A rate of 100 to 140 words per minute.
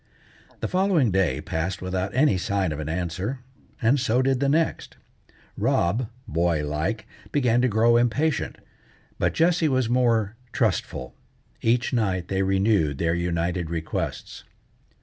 Yes: slow, 135 wpm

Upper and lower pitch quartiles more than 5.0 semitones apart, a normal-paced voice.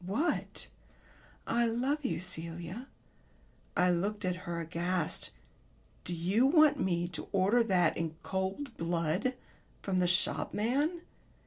No: wide, 5.6 semitones; slow, 120 wpm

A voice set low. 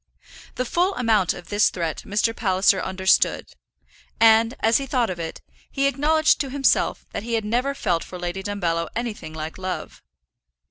No: high, 210 Hz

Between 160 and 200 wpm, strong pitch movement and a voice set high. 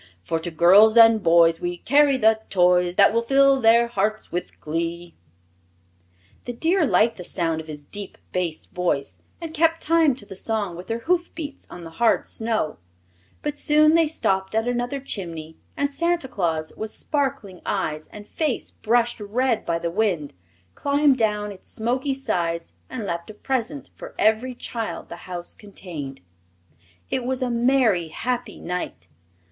Yes: average, 165 wpm; wide, 6.9 semitones; high, 220 Hz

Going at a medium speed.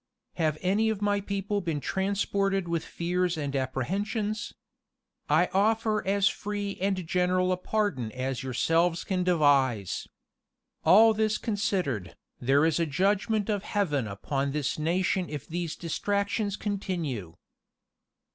No: slow, 130 wpm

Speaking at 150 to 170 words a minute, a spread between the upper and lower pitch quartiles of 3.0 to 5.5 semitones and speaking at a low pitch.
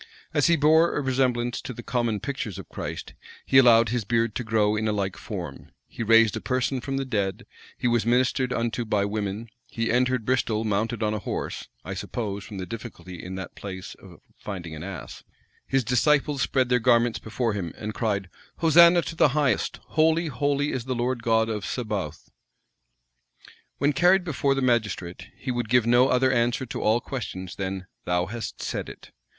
No: average, 190 wpm; average, 3.6 semitones; low, 120 Hz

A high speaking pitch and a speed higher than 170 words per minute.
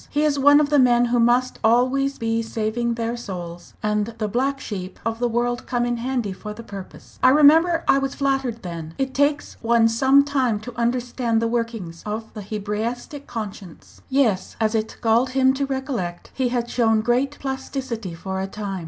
Yes: high, 235 Hz; average, 190 wpm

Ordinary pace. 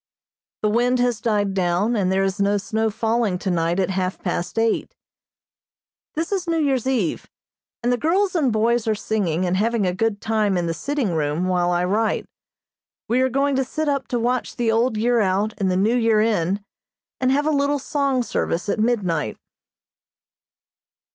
Yes: average, 185 wpm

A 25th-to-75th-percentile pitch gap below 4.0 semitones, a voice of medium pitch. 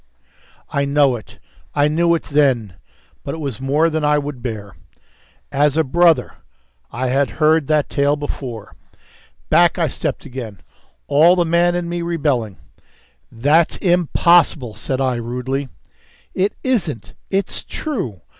No: average, 4.6 semitones; medium, 145 Hz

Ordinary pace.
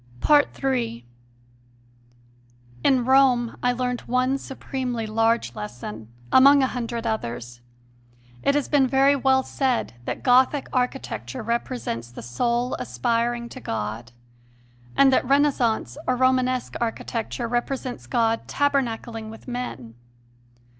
No: slow, 115 wpm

